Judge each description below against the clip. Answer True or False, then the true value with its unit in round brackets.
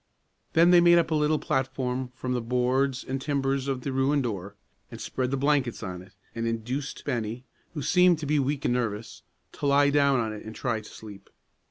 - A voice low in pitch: True (130 Hz)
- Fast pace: True (210 wpm)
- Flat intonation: False (3.6 semitones)